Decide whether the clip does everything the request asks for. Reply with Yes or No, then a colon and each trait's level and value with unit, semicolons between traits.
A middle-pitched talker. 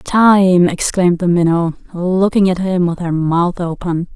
Yes: medium, 180 Hz